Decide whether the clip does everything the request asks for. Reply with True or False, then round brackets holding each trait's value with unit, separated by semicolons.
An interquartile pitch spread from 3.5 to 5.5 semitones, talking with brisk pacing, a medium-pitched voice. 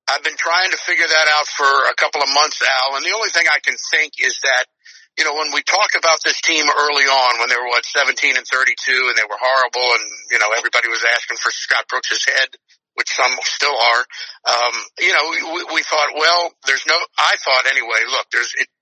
False (3.0 semitones; 230 wpm; 145 Hz)